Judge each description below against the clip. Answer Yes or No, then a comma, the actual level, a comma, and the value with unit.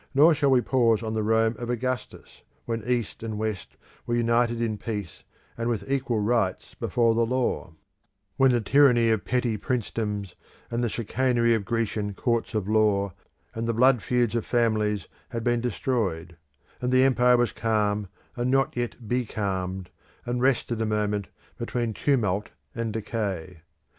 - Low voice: Yes, low, 115 Hz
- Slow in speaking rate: No, average, 160 wpm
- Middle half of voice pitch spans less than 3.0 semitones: Yes, narrow, 2.6 semitones